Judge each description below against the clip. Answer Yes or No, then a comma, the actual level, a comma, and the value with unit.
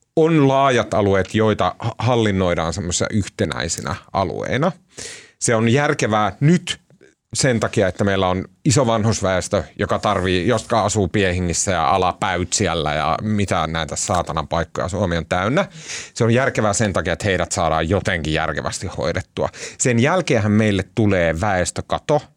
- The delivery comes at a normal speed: Yes, average, 135 wpm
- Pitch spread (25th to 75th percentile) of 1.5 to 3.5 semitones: No, average, 4.3 semitones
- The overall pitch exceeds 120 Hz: No, low, 105 Hz